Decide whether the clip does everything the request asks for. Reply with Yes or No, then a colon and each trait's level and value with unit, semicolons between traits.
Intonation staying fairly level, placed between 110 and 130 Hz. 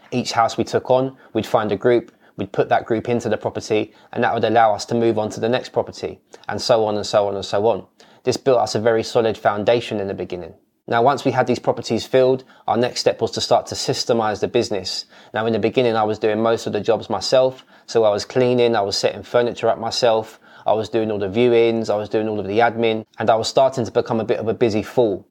Yes: narrow, 2.0 semitones; low, 115 Hz